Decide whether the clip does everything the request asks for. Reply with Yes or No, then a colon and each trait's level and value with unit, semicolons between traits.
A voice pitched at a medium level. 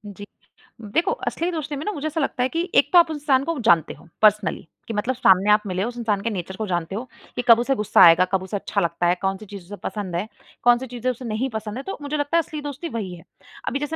No: high, 230 Hz